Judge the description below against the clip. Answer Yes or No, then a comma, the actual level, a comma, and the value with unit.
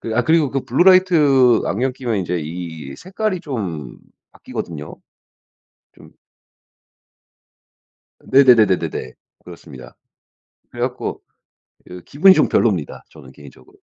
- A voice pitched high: No, low, 115 Hz